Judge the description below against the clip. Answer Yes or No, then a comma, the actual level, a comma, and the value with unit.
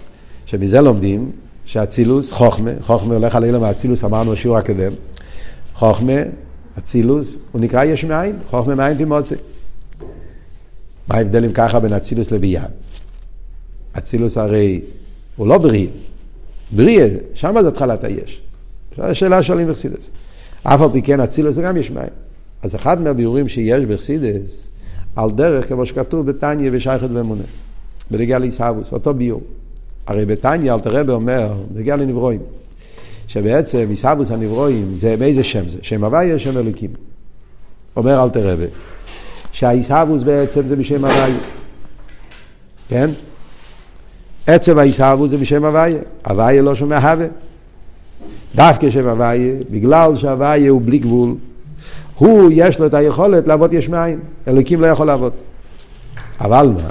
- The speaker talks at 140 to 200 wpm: No, average, 130 wpm